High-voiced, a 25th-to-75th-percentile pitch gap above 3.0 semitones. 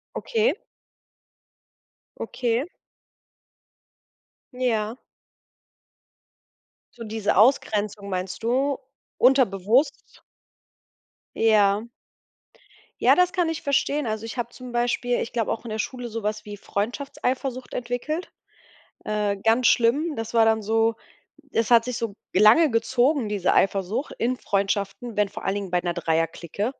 Yes: high, 230 Hz; average, 3.5 semitones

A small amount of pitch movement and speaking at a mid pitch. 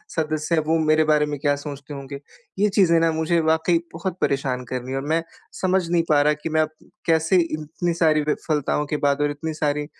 Yes: narrow, 2.1 semitones; medium, 155 Hz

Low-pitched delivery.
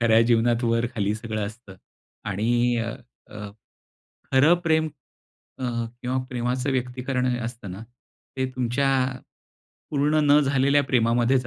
Yes: low, 120 Hz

